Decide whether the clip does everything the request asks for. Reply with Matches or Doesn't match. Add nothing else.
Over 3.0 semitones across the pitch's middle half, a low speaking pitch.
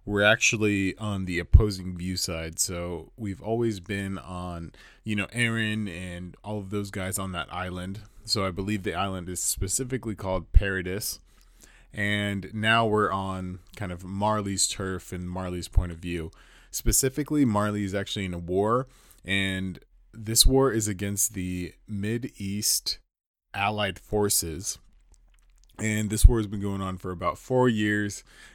Doesn't match